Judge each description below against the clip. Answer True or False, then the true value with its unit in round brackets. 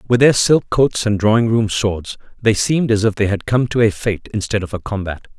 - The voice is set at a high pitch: False (110 Hz)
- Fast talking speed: True (245 wpm)